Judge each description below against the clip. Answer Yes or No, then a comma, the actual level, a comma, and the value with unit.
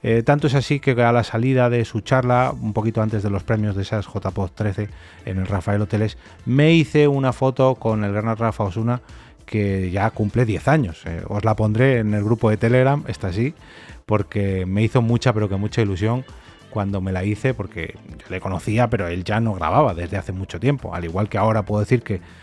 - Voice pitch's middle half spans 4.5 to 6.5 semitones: No, average, 3.5 semitones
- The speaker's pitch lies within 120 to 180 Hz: No, low, 110 Hz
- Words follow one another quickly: Yes, fast, 220 wpm